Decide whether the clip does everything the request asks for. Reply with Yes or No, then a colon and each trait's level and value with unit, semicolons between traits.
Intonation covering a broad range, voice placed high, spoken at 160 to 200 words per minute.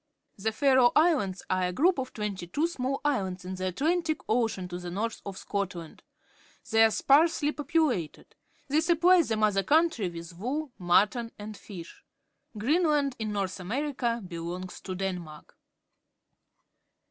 No: wide, 7.6 semitones; high, 220 Hz; average, 145 wpm